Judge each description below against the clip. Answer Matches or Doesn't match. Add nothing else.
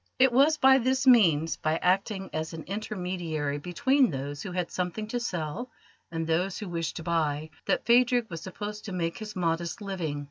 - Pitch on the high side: Doesn't match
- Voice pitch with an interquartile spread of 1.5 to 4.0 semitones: Doesn't match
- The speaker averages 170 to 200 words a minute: Matches